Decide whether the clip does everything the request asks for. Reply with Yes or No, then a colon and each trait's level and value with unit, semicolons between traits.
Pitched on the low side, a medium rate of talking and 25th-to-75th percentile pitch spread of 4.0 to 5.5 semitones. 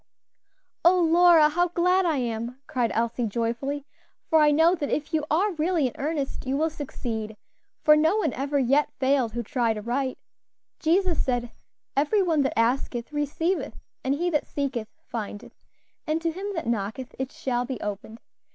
No: very high, 280 Hz; average, 170 wpm; average, 5.1 semitones